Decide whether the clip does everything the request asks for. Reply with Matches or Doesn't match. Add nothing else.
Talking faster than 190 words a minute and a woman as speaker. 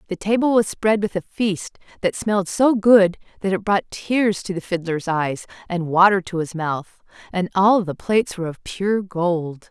Matches